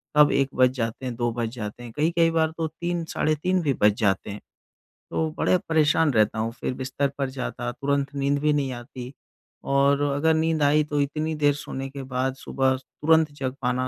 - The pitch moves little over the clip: No, average, 3.2 semitones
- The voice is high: No, medium, 140 Hz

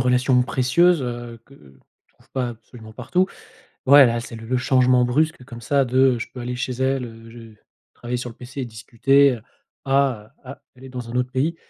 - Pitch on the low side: Yes, low, 125 Hz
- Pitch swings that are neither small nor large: No, narrow, 2.1 semitones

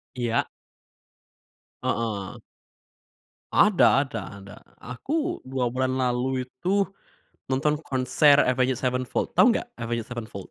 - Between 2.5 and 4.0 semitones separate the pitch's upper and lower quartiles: Yes, average, 2.9 semitones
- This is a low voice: Yes, low, 130 Hz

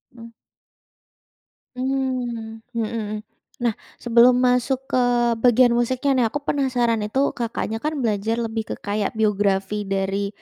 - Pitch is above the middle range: Yes, high, 235 Hz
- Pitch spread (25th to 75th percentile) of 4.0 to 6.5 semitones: No, average, 2.9 semitones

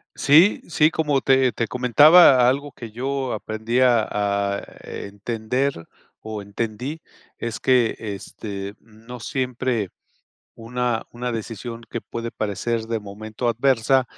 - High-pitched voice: No, low, 115 Hz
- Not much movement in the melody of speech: No, average, 3.0 semitones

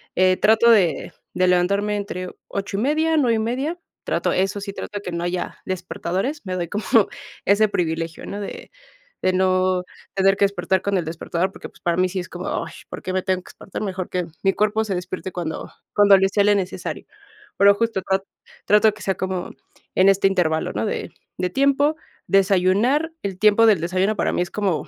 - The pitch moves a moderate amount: No, narrow, 2.3 semitones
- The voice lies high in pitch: Yes, high, 195 Hz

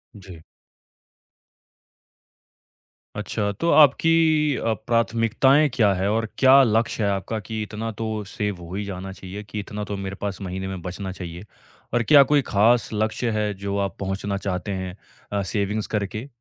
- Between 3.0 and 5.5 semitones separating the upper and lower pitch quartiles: No, narrow, 2.6 semitones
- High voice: No, low, 105 Hz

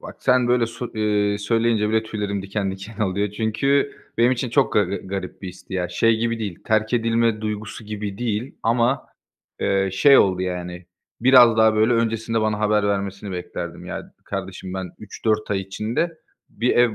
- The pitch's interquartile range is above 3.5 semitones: No, average, 2.8 semitones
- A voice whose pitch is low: Yes, low, 110 Hz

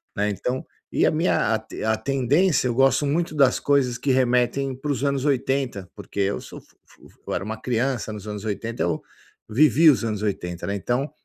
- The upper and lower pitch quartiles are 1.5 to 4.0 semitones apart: No, average, 4.5 semitones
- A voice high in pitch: No, low, 125 Hz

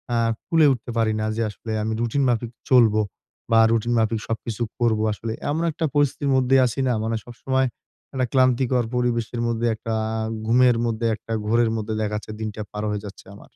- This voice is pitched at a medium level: No, low, 115 Hz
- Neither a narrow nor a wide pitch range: No, narrow, 2.3 semitones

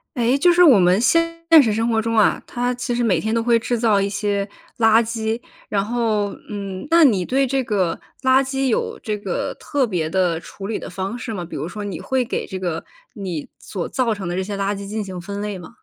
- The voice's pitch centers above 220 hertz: No, high, 215 Hz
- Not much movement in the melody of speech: No, average, 3.7 semitones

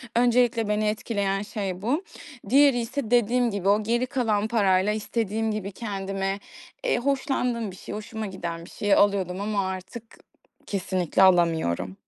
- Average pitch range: Yes, average, 3.4 semitones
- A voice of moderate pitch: No, high, 210 Hz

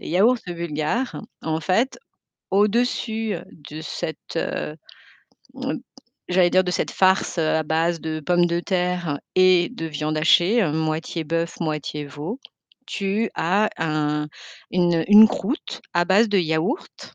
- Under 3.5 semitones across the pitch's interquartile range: No, average, 3.8 semitones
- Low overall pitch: No, medium, 175 Hz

